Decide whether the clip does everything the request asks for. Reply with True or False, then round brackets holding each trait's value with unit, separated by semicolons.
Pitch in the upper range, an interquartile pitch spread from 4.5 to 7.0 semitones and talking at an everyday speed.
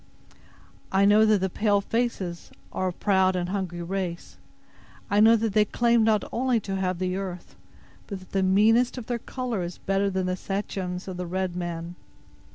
False (195 Hz; 2.8 semitones; 185 wpm)